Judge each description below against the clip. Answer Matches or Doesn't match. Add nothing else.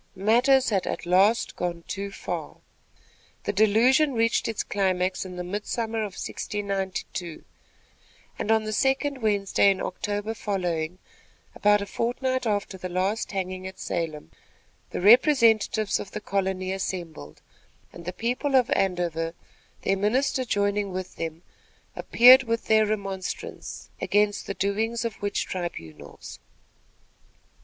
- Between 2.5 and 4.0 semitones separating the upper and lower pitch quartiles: Matches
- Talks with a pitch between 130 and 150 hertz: Doesn't match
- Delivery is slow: Matches